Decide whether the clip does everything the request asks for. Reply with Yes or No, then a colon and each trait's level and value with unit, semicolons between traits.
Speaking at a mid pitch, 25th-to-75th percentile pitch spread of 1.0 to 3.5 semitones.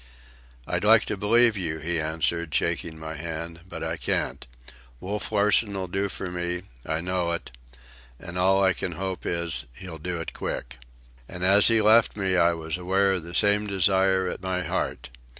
No: very low, 90 Hz; narrow, 2.6 semitones